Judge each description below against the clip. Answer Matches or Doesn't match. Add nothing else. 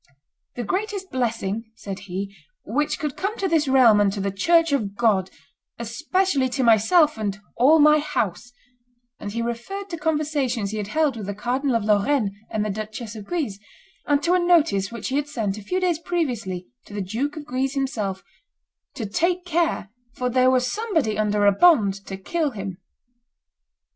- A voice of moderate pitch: Doesn't match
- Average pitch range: Doesn't match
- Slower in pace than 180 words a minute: Doesn't match